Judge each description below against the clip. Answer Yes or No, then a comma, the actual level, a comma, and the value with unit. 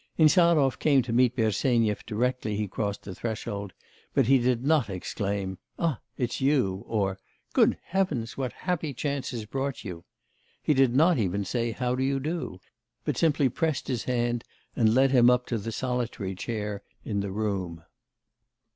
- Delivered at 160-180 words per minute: Yes, average, 165 wpm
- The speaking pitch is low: Yes, low, 120 Hz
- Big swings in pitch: No, average, 4.5 semitones